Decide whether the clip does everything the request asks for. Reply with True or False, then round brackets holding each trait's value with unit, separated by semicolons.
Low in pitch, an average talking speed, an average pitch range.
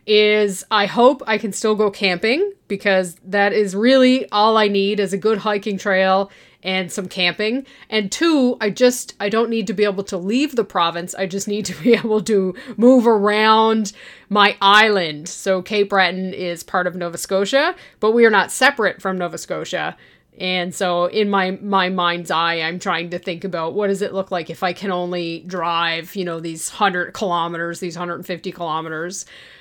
False (195 Hz; 190 wpm; 3.2 semitones)